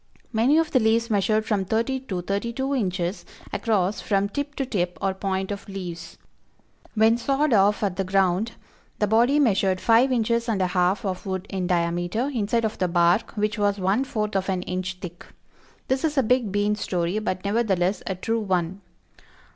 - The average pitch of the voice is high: Yes, high, 205 Hz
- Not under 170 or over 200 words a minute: Yes, average, 185 wpm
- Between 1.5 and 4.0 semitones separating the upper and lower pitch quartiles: Yes, average, 3.7 semitones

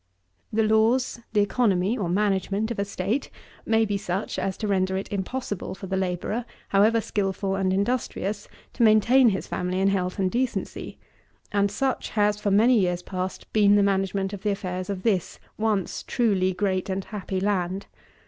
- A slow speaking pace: No, average, 175 wpm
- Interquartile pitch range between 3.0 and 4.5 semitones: No, narrow, 2.4 semitones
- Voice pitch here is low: No, high, 200 Hz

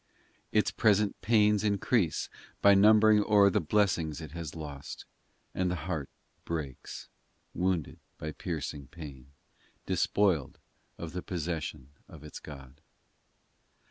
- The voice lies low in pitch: Yes, very low, 85 Hz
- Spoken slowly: Yes, slow, 125 wpm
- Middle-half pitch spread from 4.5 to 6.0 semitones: Yes, average, 5.1 semitones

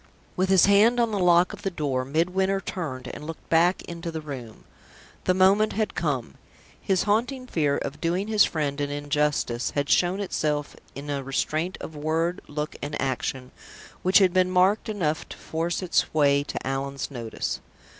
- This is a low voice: No, medium, 165 Hz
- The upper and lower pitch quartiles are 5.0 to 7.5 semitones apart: No, average, 4.6 semitones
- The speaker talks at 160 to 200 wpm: Yes, average, 175 wpm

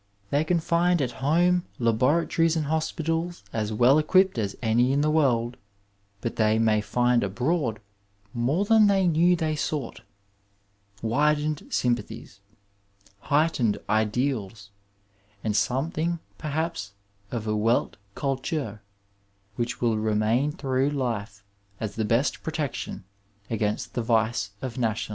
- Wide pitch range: Yes, wide, 5.9 semitones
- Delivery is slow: Yes, slow, 125 wpm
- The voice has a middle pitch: No, low, 125 Hz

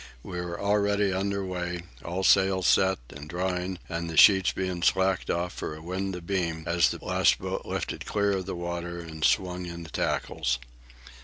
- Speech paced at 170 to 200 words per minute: Yes, average, 180 wpm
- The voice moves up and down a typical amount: No, narrow, 1.8 semitones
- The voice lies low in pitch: Yes, very low, 90 Hz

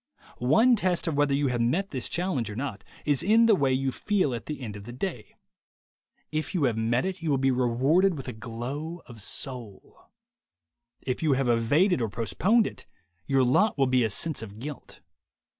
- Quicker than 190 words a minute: Yes, average, 200 wpm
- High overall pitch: No, low, 135 Hz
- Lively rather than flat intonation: Yes, wide, 5.8 semitones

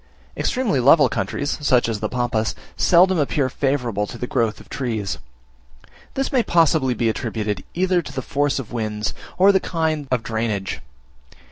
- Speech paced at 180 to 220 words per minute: No, average, 165 wpm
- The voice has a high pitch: No, low, 130 Hz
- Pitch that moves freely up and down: Yes, wide, 6.0 semitones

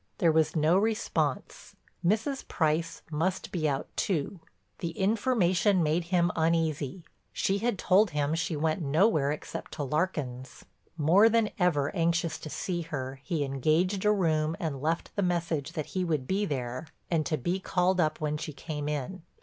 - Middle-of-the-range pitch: Yes, medium, 165 Hz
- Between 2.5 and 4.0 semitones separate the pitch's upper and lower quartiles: Yes, average, 3.6 semitones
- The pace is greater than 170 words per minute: No, average, 165 wpm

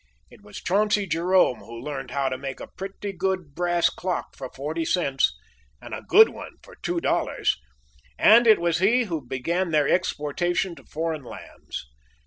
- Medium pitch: Yes, medium, 175 Hz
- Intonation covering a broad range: No, average, 5.0 semitones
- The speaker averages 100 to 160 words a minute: No, average, 170 wpm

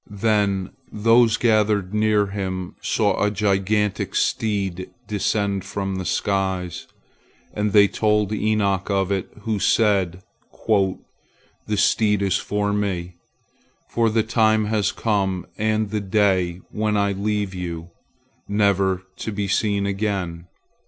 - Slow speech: Yes, slow, 125 wpm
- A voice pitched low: Yes, low, 100 Hz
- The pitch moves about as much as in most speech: No, narrow, 1.8 semitones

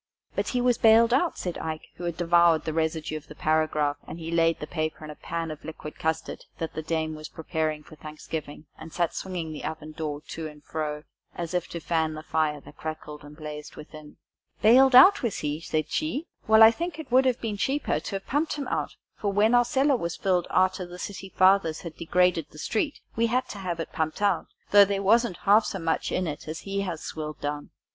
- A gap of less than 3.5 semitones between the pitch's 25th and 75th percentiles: No, average, 4.6 semitones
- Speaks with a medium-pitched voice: Yes, medium, 165 Hz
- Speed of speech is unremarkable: No, fast, 230 wpm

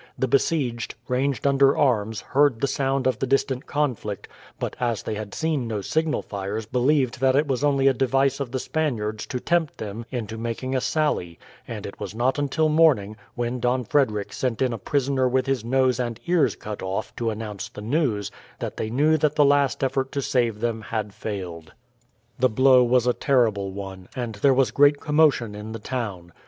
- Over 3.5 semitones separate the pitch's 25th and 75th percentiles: Yes, average, 4.1 semitones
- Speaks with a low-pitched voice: Yes, low, 125 Hz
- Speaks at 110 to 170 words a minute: No, average, 195 wpm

